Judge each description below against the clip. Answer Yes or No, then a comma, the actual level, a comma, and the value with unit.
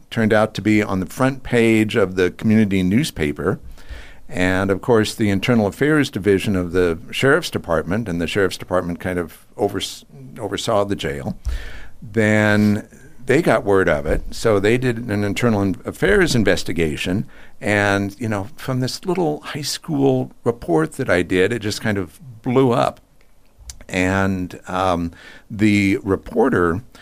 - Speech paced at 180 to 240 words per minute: No, average, 155 wpm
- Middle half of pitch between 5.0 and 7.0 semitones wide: No, average, 4.3 semitones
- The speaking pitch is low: Yes, low, 105 Hz